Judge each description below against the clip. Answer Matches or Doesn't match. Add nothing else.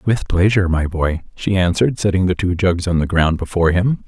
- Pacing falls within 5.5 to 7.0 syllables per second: Matches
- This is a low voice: Matches